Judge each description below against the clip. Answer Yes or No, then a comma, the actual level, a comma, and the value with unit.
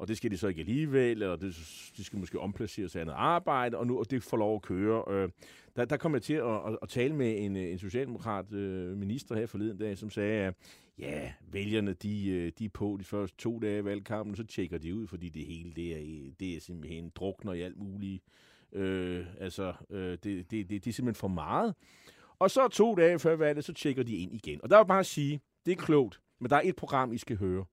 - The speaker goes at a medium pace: No, fast, 235 wpm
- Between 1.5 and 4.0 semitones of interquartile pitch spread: No, average, 4.6 semitones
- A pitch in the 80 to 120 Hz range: Yes, low, 105 Hz